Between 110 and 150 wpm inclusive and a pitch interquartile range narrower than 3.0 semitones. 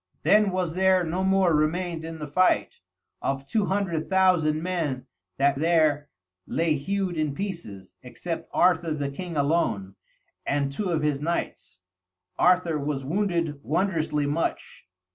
No: average, 140 wpm; average, 3.9 semitones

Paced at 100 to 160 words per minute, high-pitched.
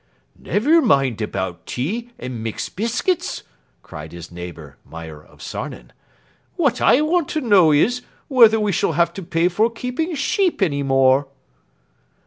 No: average, 145 wpm; medium, 170 Hz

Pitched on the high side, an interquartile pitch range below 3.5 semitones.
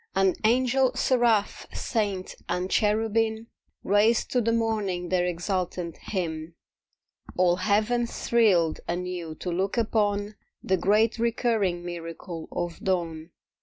No: high, 195 Hz; average, 4.1 semitones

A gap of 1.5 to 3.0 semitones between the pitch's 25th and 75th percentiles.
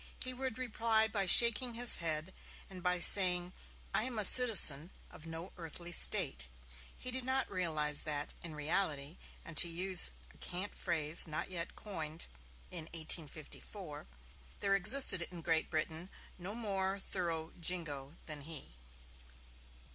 No: average, 4.1 semitones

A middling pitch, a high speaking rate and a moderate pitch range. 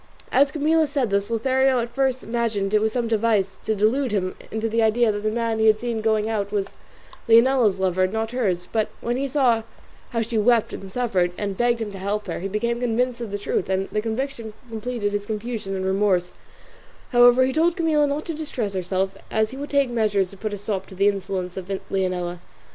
No: high, 220 Hz; fast, 220 wpm; average, 3.6 semitones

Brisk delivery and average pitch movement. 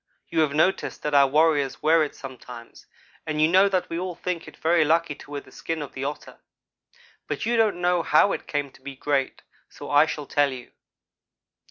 Yes: fast, 210 wpm; average, 3.1 semitones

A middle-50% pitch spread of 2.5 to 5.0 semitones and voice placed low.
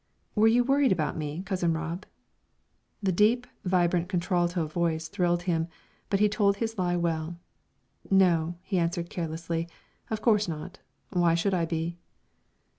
No: average, 2.9 semitones; medium, 175 Hz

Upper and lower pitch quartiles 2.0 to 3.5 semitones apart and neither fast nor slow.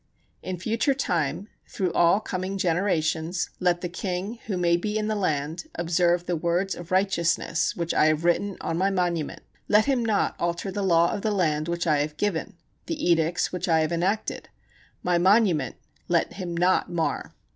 Yes: narrow, 2.6 semitones; average, 180 wpm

